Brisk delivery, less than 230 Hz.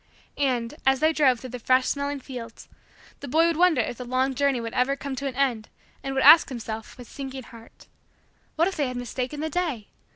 No: fast, 220 wpm; very high, 265 Hz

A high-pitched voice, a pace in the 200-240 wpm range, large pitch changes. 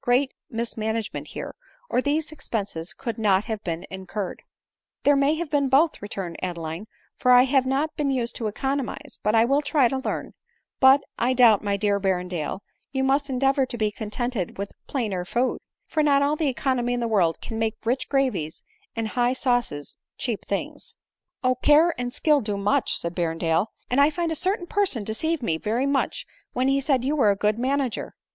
No: high, 245 Hz; fast, 205 wpm; average, 5.0 semitones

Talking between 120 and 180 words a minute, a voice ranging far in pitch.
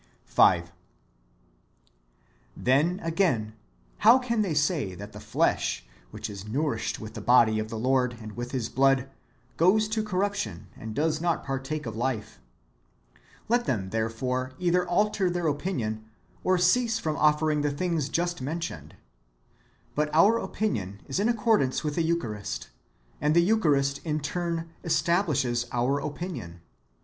Yes: average, 145 wpm; wide, 6.6 semitones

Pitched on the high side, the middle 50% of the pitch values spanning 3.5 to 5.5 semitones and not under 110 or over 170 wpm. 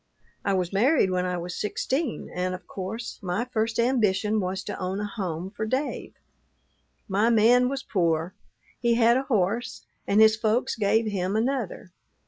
Yes: high, 210 Hz; average, 4.0 semitones; average, 165 wpm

